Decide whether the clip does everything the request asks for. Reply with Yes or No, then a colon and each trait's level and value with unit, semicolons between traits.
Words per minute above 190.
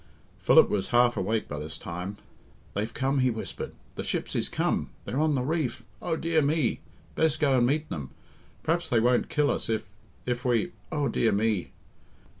No: average, 185 wpm